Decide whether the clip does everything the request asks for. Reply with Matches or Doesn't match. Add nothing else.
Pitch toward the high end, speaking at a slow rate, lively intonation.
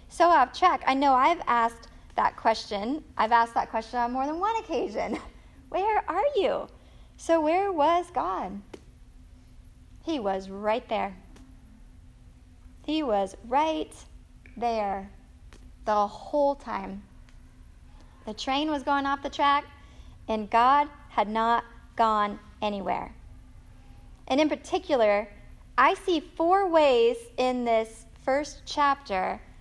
Matches